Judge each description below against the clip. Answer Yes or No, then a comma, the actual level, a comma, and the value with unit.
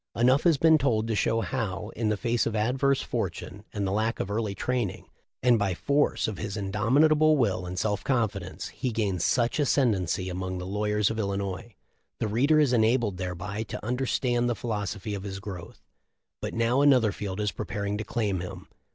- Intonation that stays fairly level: No, average, 3.8 semitones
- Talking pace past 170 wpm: Yes, average, 185 wpm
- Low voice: Yes, low, 110 Hz